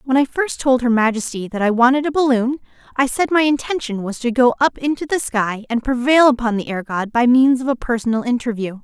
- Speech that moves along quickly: Yes, fast, 230 wpm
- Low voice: No, very high, 250 Hz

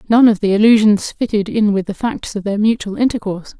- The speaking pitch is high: Yes, high, 210 Hz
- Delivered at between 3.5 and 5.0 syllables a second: No, 5.9 syllables/s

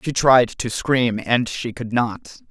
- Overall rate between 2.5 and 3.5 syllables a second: Yes, 3.4 syllables/s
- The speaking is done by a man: Yes, male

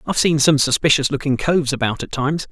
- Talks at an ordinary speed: No, fast, 215 wpm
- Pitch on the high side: No, medium, 140 Hz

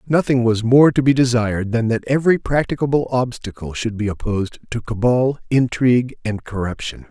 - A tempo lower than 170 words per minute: Yes, average, 160 wpm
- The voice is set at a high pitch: No, low, 120 Hz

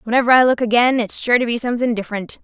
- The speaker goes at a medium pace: No, fast, 245 wpm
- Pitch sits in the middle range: No, high, 235 Hz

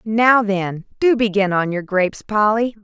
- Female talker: Yes, female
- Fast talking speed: No, average, 170 wpm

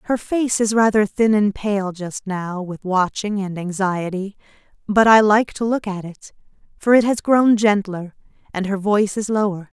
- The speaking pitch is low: No, high, 205 Hz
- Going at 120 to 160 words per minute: No, average, 185 wpm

